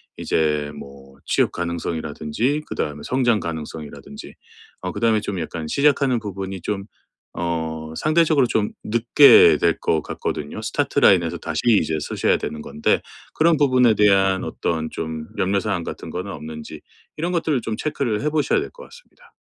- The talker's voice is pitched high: No, very low, 95 Hz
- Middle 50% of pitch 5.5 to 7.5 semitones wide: No, wide, 8.2 semitones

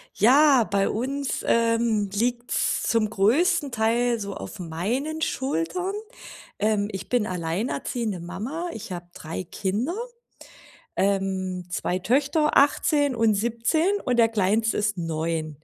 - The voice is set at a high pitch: Yes, high, 220 Hz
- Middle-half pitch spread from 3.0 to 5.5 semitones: Yes, average, 5.1 semitones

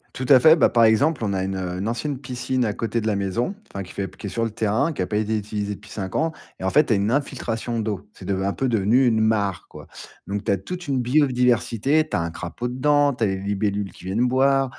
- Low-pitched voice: Yes, low, 110 Hz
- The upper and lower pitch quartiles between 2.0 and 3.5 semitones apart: No, average, 4.5 semitones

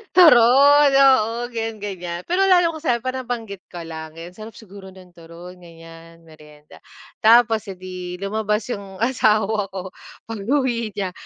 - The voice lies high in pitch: Yes, high, 210 Hz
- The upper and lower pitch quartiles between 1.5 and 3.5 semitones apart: No, average, 5.2 semitones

